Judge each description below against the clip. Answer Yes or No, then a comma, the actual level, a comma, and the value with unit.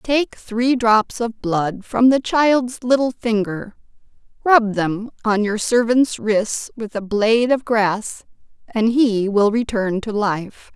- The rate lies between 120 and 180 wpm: Yes, average, 150 wpm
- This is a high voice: Yes, high, 225 Hz